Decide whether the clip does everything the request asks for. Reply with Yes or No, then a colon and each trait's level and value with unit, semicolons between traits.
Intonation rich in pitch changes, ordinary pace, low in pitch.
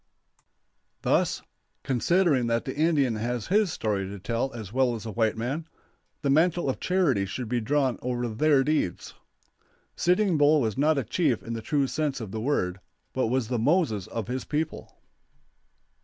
No: average, 5.0 semitones; average, 170 wpm; low, 130 Hz